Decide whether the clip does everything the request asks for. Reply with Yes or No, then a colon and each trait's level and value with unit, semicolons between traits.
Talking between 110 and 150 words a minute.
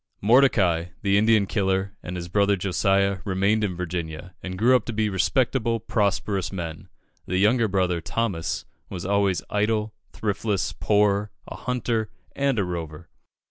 Yes: average, 145 wpm